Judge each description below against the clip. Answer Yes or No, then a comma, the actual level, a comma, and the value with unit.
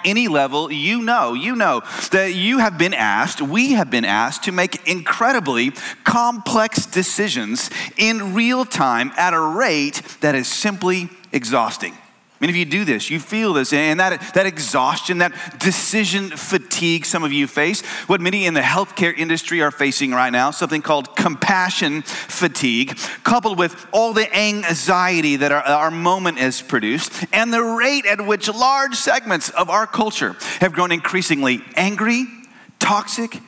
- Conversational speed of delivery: Yes, average, 160 wpm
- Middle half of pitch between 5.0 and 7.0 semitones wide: Yes, average, 5.3 semitones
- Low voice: No, medium, 185 Hz